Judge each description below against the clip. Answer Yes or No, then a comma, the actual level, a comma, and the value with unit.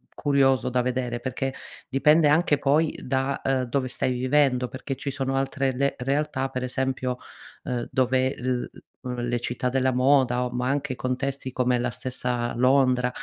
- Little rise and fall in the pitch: Yes, narrow, 1.4 semitones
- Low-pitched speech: Yes, low, 130 Hz